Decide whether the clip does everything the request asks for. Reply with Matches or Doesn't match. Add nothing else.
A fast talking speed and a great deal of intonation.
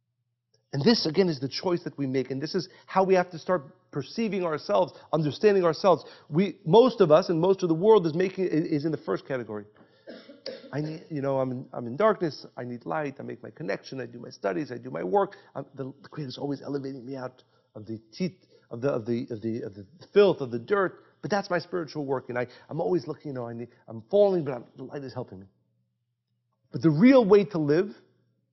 Matches